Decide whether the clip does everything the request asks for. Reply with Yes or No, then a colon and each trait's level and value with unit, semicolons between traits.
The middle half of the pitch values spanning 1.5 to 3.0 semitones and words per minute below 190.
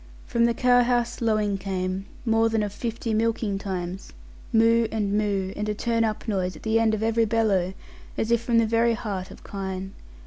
No: average, 2.7 semitones; average, 195 wpm